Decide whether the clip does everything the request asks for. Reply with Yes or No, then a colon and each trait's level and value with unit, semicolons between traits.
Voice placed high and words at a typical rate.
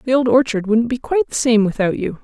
No: high, 240 Hz; fast, 270 wpm